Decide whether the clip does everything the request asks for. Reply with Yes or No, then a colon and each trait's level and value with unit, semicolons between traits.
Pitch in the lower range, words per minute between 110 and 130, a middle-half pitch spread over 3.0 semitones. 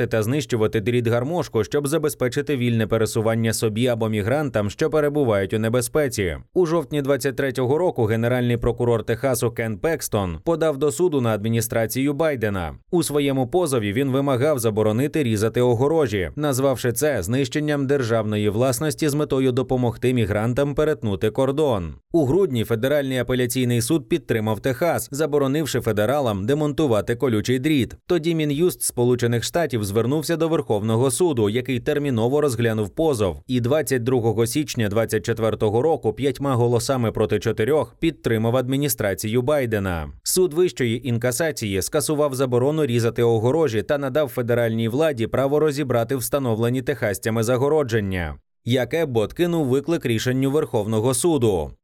Yes: low, 125 Hz; average, 125 wpm; average, 4.6 semitones